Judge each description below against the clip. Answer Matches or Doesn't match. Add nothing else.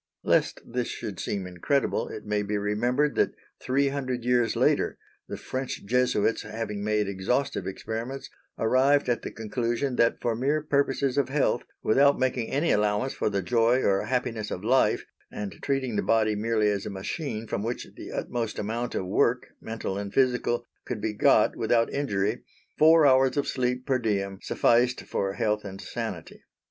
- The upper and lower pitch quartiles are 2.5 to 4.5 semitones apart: Matches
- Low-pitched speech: Matches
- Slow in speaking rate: Doesn't match